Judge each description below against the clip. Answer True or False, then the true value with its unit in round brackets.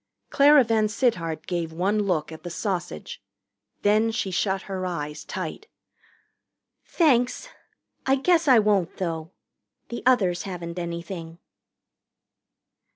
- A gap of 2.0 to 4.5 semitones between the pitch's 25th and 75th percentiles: False (5.1 semitones)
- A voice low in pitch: False (190 Hz)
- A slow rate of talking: True (110 wpm)